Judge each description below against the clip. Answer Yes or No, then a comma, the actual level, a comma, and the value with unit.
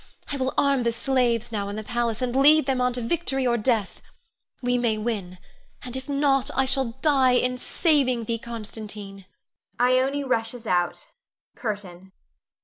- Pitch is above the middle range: Yes, high, 245 Hz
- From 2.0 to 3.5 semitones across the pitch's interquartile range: Yes, average, 3.2 semitones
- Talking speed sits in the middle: Yes, average, 160 wpm